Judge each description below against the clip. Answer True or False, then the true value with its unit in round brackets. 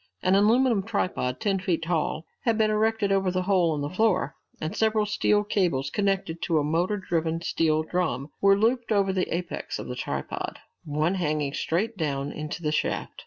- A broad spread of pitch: False (4.7 semitones)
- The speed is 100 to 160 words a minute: False (185 wpm)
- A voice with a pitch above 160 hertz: True (185 Hz)